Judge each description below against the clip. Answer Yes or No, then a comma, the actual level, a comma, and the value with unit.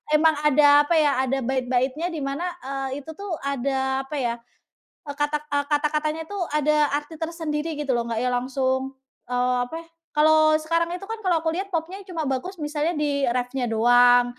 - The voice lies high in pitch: Yes, very high, 295 Hz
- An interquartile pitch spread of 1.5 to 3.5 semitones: Yes, average, 3.2 semitones